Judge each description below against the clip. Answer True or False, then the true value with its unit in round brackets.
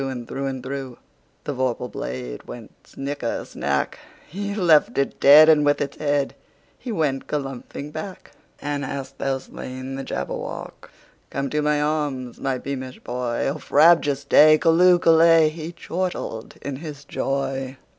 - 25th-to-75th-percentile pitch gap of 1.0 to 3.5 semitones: True (2.8 semitones)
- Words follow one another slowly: True (125 wpm)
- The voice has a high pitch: False (140 Hz)